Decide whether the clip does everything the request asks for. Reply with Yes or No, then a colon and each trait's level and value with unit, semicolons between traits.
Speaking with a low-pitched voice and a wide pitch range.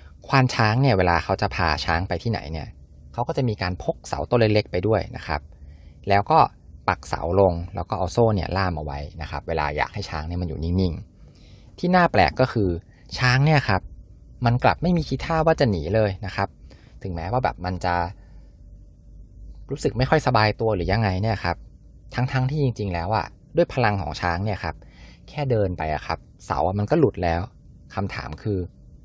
Yes: very low, 95 Hz; wide, 5.7 semitones